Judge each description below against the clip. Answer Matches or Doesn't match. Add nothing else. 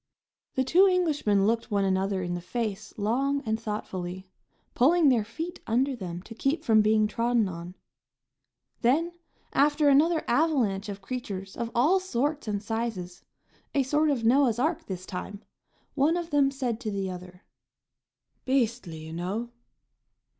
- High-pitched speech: Matches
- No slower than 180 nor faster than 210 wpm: Doesn't match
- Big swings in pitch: Matches